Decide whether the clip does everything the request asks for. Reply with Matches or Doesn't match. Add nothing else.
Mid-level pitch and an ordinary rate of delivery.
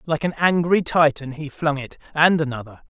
Matches